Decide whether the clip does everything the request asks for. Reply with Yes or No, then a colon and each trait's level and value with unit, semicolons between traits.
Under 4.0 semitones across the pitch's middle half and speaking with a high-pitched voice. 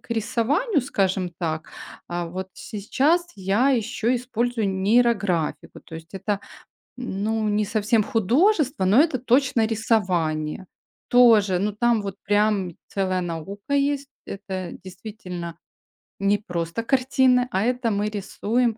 No: average, 4.5 semitones; high, 210 Hz